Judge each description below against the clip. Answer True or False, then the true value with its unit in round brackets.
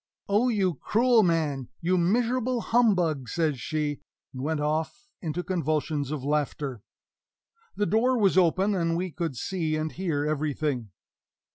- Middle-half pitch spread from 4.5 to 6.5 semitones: True (4.9 semitones)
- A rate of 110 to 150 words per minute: True (140 wpm)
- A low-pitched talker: False (165 Hz)